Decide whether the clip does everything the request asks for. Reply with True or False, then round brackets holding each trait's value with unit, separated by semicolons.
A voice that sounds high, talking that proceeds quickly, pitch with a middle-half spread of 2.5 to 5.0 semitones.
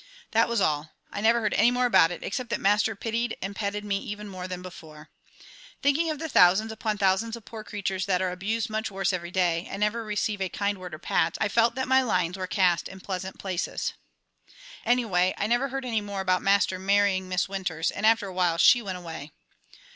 True (200 Hz; 215 wpm; 3.4 semitones)